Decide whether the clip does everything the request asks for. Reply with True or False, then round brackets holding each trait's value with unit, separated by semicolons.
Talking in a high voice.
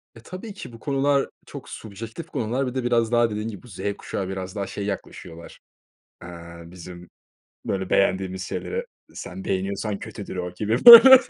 False (110 Hz)